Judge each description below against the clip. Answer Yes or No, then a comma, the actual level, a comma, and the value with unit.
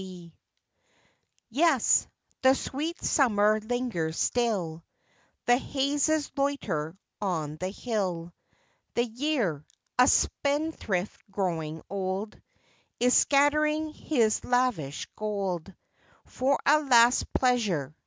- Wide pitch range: Yes, wide, 7.1 semitones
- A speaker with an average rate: No, slow, 90 wpm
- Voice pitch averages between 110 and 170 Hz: No, high, 230 Hz